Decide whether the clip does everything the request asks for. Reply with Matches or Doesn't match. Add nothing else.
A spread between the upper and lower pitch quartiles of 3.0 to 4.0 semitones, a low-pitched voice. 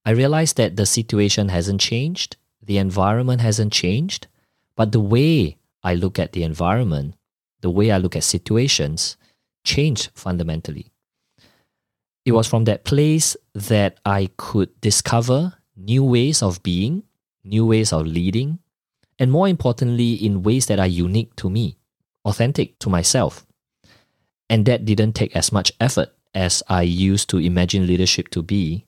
Doesn't match